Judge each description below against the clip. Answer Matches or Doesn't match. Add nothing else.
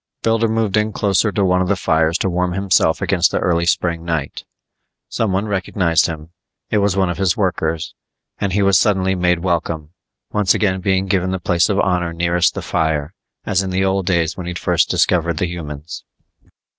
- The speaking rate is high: Doesn't match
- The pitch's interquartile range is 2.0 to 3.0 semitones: Matches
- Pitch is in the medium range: Doesn't match